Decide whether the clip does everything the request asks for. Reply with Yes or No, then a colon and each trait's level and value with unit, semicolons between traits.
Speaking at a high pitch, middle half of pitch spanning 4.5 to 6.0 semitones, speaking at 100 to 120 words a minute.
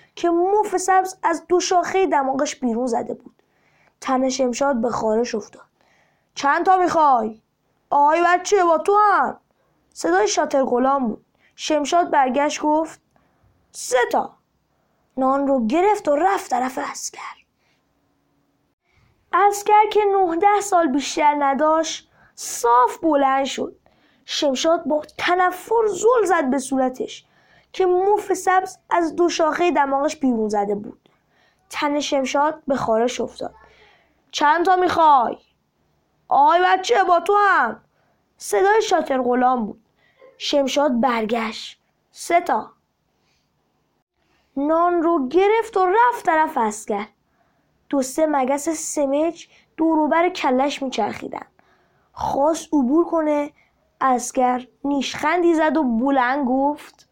Yes: very high, 310 Hz; average, 5.2 semitones; average, 115 wpm